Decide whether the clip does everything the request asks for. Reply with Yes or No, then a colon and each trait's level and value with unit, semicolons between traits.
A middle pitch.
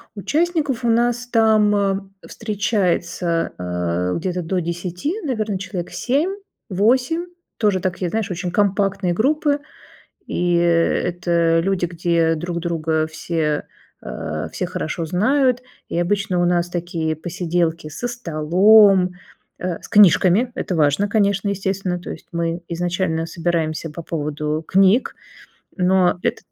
Yes: medium, 180 Hz